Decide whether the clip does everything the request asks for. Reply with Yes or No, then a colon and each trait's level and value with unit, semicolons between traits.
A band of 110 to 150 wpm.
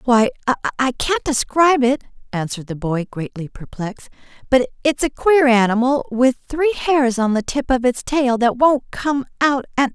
No: average, 170 wpm